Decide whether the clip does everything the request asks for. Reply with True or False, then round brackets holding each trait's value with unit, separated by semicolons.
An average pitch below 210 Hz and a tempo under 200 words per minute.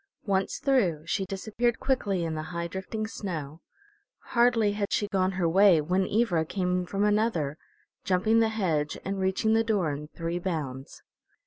True (190 Hz; 160 wpm)